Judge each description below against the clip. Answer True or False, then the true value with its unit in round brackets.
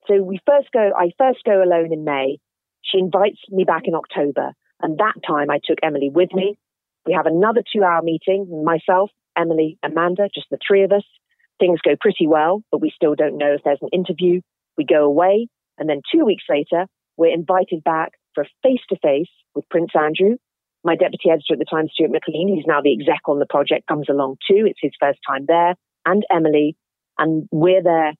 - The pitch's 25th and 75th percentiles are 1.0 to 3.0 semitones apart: False (4.2 semitones)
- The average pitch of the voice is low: False (170 Hz)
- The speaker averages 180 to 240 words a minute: True (200 wpm)